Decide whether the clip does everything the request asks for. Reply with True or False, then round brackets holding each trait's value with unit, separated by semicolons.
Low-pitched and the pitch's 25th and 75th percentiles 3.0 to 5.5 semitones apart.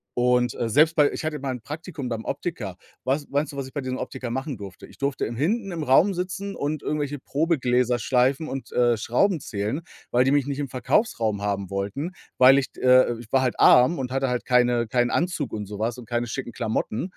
True (130 Hz; 3.5 semitones)